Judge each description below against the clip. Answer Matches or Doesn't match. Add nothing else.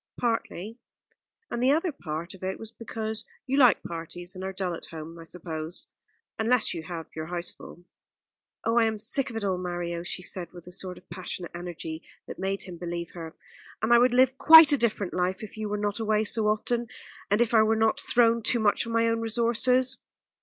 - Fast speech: Matches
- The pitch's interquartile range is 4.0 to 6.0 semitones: Matches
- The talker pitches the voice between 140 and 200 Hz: Doesn't match